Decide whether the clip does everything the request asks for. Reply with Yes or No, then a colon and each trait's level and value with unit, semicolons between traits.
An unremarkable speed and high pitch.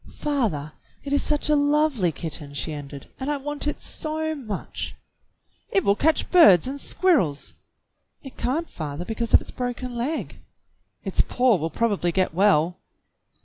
Yes: average, 155 wpm; high, 245 Hz